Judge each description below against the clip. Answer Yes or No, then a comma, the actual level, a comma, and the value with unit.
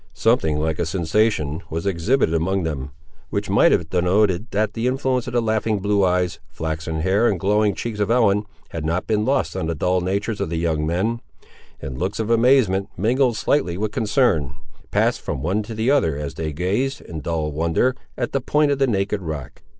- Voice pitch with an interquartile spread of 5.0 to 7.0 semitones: Yes, wide, 5.6 semitones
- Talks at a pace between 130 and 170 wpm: No, average, 200 wpm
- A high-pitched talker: No, low, 100 Hz